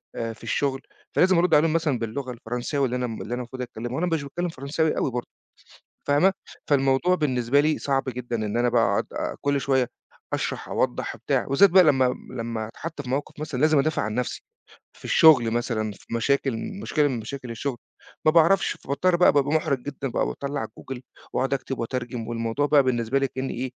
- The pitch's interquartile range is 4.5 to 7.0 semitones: No, average, 3.4 semitones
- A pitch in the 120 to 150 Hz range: Yes, low, 135 Hz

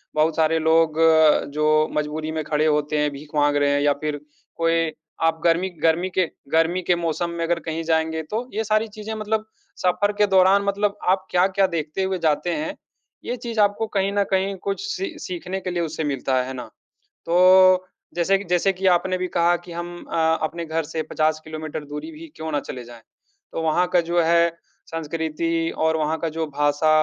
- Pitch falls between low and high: Yes, medium, 165 Hz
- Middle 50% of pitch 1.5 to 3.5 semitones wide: Yes, average, 3.1 semitones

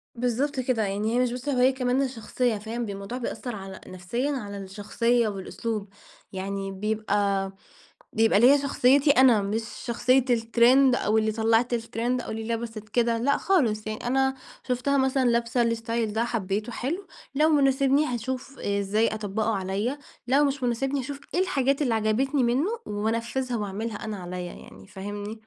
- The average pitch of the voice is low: No, high, 230 Hz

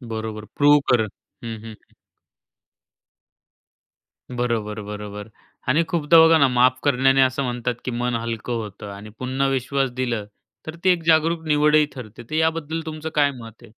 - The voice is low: Yes, low, 130 Hz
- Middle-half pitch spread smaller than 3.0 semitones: No, average, 4.7 semitones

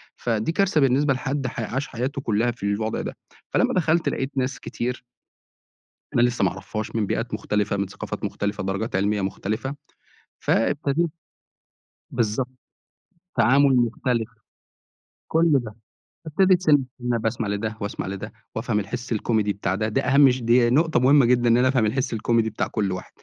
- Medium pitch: No, low, 120 Hz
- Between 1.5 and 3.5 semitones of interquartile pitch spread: No, average, 4.0 semitones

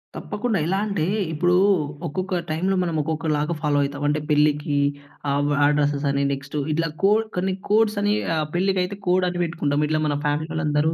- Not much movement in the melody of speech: No, average, 4.0 semitones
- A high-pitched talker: No, medium, 160 Hz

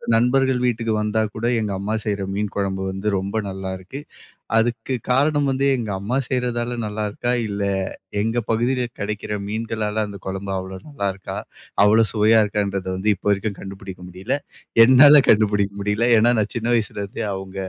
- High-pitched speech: No, low, 105 Hz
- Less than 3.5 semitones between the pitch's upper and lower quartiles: Yes, average, 3.0 semitones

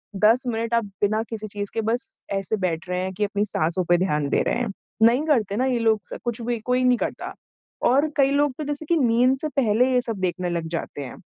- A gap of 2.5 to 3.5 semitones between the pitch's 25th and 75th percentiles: No, average, 4.3 semitones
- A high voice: Yes, high, 225 Hz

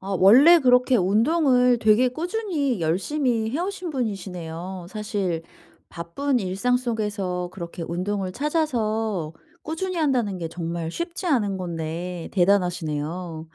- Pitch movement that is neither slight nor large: No, wide, 6.5 semitones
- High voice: Yes, high, 205 Hz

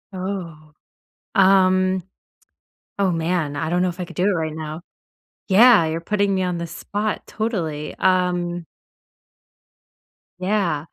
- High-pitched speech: No, medium, 180 Hz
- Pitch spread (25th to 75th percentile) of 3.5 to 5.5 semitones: No, average, 2.8 semitones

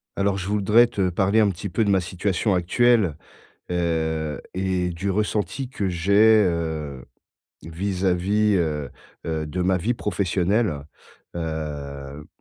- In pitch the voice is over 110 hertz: No, very low, 90 Hz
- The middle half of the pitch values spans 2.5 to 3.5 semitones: No, average, 3.9 semitones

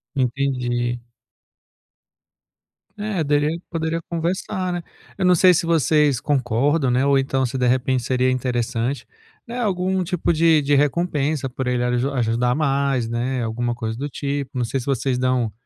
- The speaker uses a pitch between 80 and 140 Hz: Yes, low, 135 Hz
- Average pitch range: Yes, average, 4.5 semitones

